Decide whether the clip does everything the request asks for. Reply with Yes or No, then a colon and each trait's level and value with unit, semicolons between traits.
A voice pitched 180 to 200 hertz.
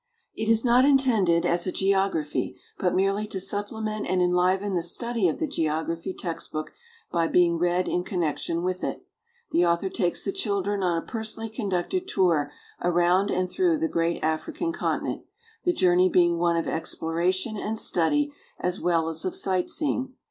Yes: medium, 185 Hz